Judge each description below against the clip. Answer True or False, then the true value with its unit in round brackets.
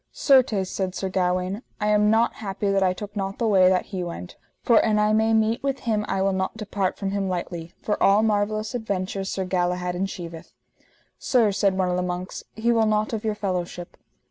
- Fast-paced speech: True (210 wpm)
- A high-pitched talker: True (195 Hz)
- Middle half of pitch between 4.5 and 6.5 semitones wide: False (2.7 semitones)